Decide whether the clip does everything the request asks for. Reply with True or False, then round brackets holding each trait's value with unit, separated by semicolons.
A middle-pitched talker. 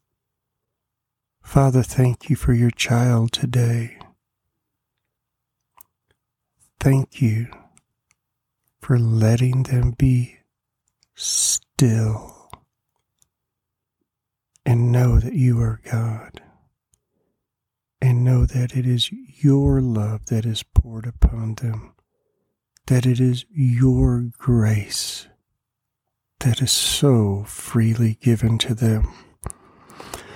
False (120 Hz)